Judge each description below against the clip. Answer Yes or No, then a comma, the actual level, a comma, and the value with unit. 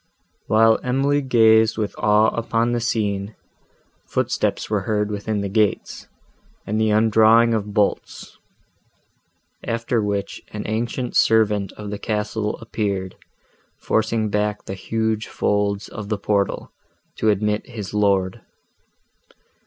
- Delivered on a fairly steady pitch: Yes, narrow, 1.5 semitones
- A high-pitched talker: No, low, 105 Hz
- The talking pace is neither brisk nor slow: No, slow, 120 wpm